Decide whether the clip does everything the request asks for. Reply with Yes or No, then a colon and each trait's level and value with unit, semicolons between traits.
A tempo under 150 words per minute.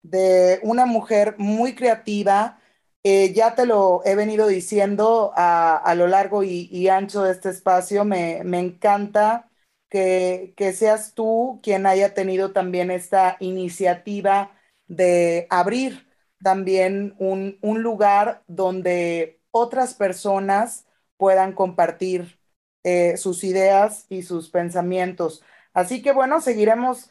Yes: slow, 125 wpm